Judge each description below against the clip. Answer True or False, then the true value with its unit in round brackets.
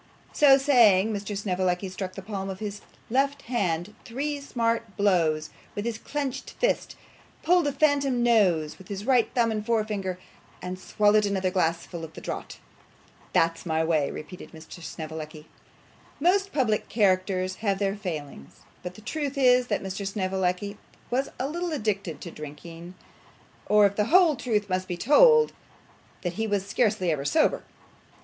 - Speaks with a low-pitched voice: False (205 Hz)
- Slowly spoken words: False (155 wpm)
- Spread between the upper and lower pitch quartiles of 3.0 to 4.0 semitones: False (5.1 semitones)